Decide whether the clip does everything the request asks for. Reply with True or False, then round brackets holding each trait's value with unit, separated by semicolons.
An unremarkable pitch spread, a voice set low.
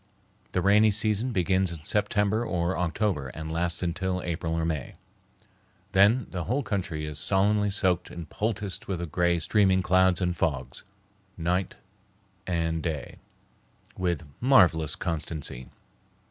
True (3.5 semitones; 90 Hz)